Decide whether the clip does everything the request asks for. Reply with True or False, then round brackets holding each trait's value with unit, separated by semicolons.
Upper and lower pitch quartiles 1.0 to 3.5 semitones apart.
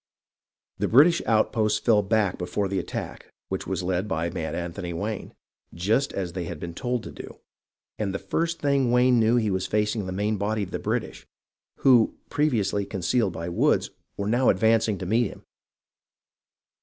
False (3.9 semitones)